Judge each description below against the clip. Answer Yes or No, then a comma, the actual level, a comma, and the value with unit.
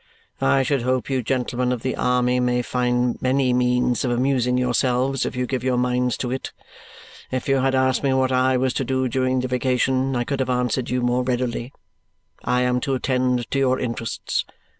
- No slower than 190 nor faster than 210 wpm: Yes, average, 200 wpm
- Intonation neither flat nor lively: No, narrow, 0.9 semitones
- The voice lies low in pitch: Yes, low, 125 Hz